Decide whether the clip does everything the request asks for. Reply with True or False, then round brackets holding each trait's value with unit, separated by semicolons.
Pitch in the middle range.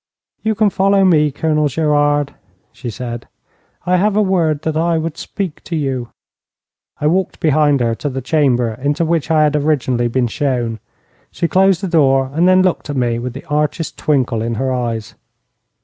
True (150 Hz)